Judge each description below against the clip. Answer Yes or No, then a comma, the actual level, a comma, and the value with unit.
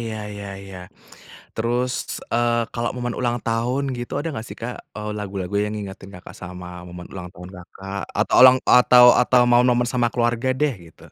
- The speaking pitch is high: No, low, 115 Hz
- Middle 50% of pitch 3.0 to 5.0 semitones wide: Yes, average, 3.9 semitones